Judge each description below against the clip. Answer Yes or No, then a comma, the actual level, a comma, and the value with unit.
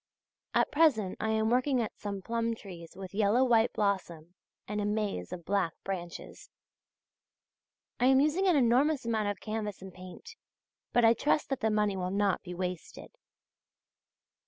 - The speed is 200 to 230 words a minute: No, average, 160 wpm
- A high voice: Yes, high, 210 Hz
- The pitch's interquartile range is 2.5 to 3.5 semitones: No, average, 4.1 semitones